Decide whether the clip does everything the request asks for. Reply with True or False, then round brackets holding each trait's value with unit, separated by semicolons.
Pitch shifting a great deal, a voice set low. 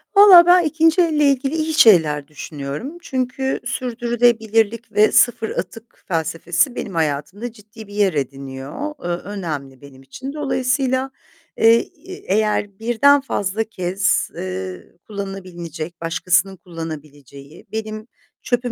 False (7.5 semitones; 210 Hz)